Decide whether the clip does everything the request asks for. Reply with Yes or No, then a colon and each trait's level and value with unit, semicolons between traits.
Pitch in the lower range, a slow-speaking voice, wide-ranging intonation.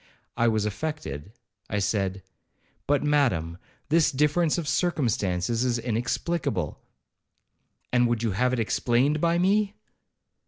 Yes: low, 120 Hz; slow, 115 wpm; wide, 6.5 semitones